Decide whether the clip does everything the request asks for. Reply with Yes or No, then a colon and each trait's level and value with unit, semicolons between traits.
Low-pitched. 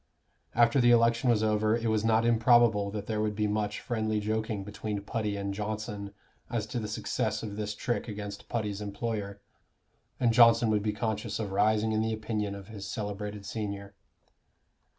Yes: low, 110 Hz